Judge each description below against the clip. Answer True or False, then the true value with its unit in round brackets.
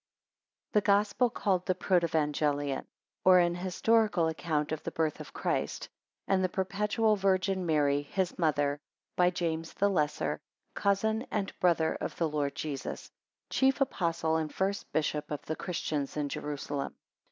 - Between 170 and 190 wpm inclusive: False (150 wpm)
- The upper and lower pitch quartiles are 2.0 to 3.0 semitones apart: False (4.4 semitones)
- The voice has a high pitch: False (170 Hz)